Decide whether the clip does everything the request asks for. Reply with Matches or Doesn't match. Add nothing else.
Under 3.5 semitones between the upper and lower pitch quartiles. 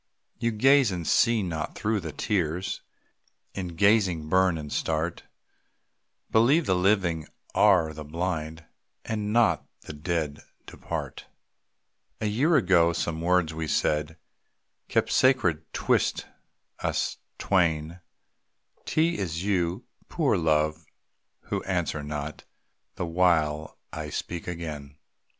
Doesn't match